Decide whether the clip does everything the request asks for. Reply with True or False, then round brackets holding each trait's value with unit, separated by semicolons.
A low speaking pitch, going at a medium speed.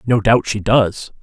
True (110 Hz; 195 wpm)